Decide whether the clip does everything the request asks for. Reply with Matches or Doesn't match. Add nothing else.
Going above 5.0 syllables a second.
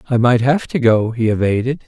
Matches